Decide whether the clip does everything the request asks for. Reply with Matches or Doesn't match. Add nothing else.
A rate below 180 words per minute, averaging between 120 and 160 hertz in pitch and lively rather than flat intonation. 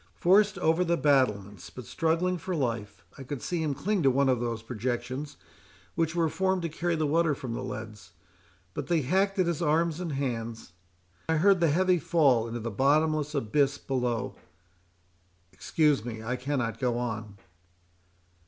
Matches